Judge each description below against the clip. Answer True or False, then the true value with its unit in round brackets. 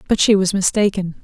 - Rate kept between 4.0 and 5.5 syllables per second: False (5.8 syllables/s)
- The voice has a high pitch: True (195 Hz)